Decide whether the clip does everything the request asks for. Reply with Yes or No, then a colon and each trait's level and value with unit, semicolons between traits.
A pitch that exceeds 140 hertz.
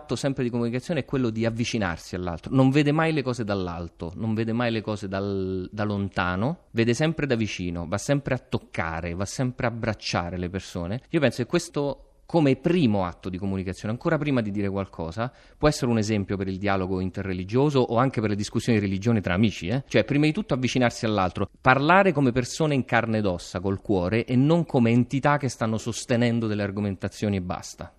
No: low, 115 Hz